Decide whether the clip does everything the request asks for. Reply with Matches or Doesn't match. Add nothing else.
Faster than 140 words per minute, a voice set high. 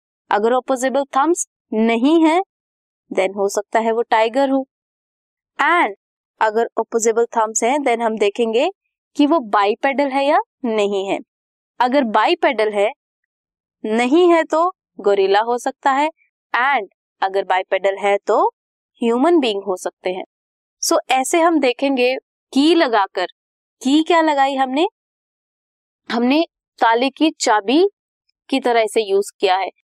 Doesn't match